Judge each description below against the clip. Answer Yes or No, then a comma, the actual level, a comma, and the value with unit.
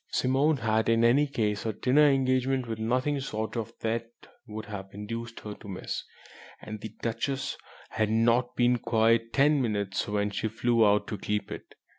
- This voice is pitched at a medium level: No, low, 115 Hz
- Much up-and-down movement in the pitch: No, average, 3.0 semitones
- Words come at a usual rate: Yes, average, 180 wpm